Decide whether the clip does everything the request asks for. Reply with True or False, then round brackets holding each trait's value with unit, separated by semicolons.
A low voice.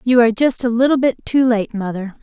False (235 Hz)